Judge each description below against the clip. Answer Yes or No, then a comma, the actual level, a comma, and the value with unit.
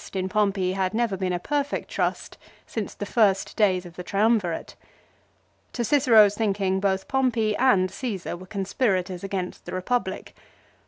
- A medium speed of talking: Yes, average, 160 wpm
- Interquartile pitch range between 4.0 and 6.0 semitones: No, average, 3.3 semitones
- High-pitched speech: Yes, high, 200 Hz